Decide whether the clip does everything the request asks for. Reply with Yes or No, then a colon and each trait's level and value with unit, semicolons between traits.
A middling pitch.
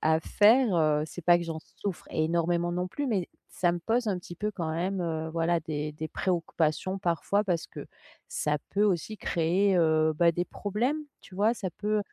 Yes: medium, 175 Hz